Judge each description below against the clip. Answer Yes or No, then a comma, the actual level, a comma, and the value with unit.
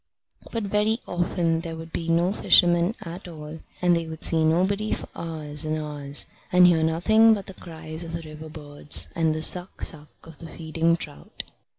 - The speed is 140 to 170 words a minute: No, average, 190 wpm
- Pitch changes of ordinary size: No, narrow, 2.1 semitones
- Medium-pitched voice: Yes, medium, 165 Hz